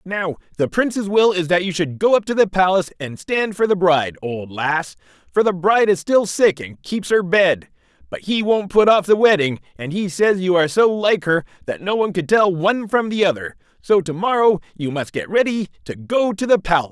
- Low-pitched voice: No, medium, 185 Hz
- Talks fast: Yes, fast, 235 wpm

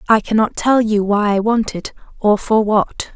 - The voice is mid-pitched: No, high, 215 Hz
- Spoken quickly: Yes, fast, 210 wpm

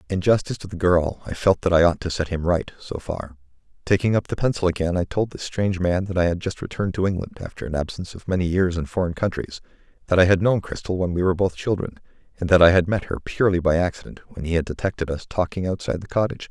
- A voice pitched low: Yes, very low, 90 Hz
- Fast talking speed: Yes, fast, 245 wpm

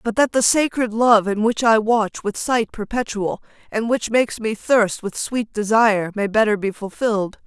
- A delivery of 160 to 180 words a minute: No, average, 195 wpm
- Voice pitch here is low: No, high, 220 Hz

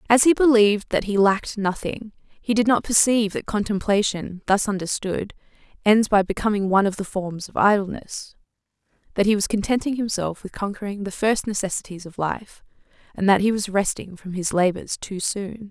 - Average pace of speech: Yes, average, 175 wpm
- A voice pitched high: Yes, high, 205 Hz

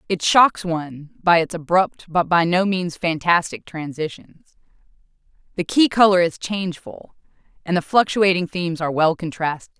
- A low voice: No, medium, 170 Hz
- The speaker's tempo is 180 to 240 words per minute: No, average, 145 wpm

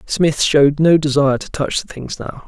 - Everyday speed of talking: No, fast, 220 wpm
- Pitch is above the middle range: No, medium, 145 Hz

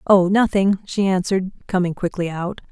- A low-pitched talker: No, high, 190 Hz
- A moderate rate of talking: Yes, average, 155 wpm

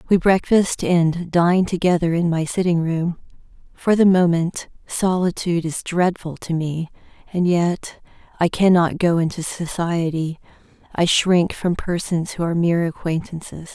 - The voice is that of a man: No, female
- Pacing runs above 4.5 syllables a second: No, 4.4 syllables/s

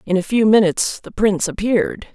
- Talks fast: No, average, 195 wpm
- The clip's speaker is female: Yes, female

